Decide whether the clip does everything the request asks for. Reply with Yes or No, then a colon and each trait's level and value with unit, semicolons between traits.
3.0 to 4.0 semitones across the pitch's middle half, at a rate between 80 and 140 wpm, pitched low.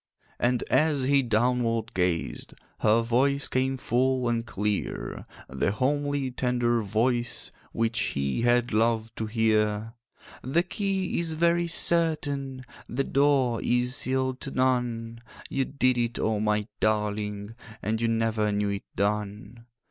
Yes: average, 3.5 semitones; slow, 135 wpm; low, 120 Hz